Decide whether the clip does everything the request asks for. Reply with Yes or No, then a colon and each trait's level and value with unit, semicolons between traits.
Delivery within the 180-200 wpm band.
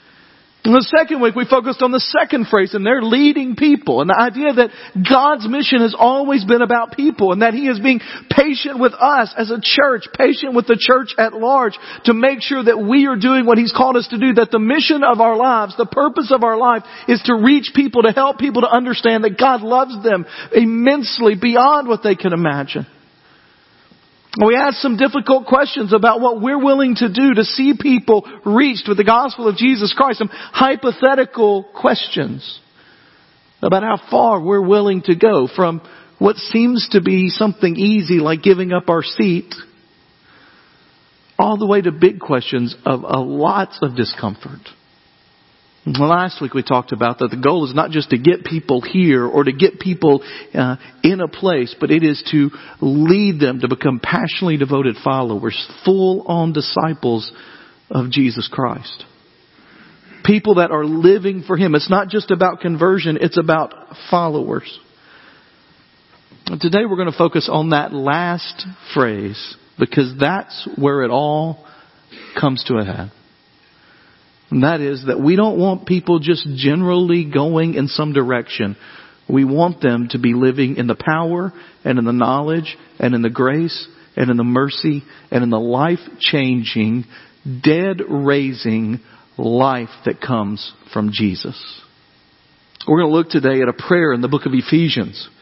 No: average, 170 wpm